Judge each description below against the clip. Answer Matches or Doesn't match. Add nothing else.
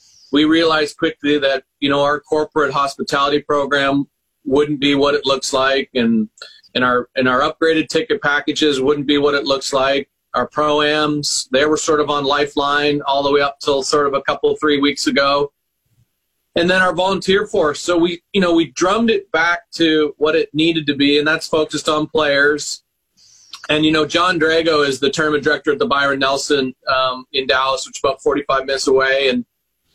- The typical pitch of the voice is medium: Matches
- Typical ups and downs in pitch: Doesn't match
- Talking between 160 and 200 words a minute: Matches